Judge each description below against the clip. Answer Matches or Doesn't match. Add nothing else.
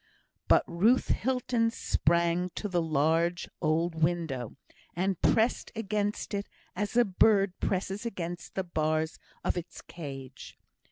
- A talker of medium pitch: Matches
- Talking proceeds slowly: Matches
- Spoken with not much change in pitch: Doesn't match